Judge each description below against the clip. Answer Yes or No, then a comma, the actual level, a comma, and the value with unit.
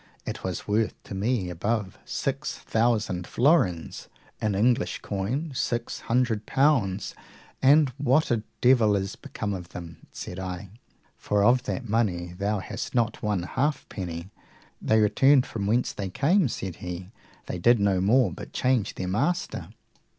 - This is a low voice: Yes, low, 105 Hz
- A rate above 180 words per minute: No, average, 150 wpm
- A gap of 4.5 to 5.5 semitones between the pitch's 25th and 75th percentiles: Yes, average, 4.9 semitones